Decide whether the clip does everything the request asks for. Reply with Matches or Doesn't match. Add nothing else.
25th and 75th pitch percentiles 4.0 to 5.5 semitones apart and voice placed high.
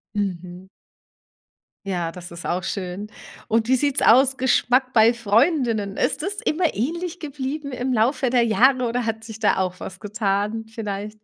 Matches